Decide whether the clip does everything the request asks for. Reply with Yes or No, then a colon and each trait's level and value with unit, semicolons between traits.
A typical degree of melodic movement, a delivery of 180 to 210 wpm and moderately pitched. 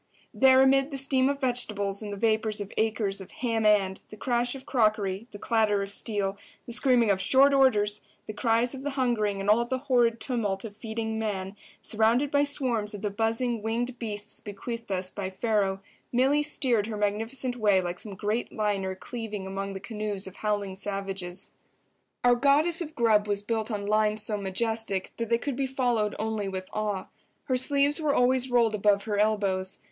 No: average, 3.3 semitones; average, 190 wpm; high, 220 Hz